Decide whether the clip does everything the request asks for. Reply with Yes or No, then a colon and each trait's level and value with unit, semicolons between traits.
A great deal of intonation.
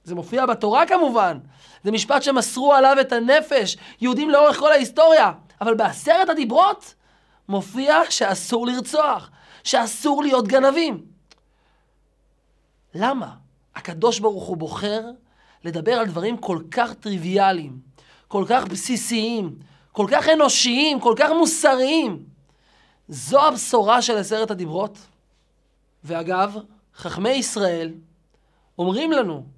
Yes: wide, 6.9 semitones